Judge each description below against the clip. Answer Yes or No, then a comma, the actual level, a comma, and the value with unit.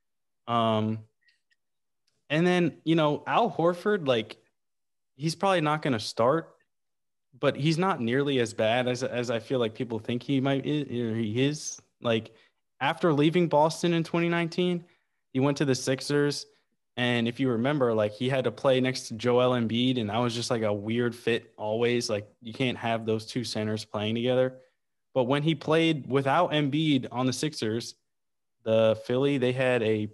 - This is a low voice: Yes, low, 130 Hz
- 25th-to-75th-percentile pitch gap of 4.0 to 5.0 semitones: Yes, average, 4.3 semitones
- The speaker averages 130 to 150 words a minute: No, average, 175 wpm